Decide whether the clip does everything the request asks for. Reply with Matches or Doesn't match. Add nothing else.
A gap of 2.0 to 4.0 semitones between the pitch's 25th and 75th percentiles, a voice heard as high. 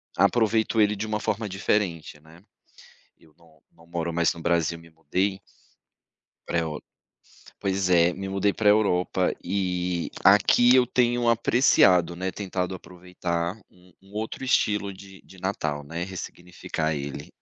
Doesn't match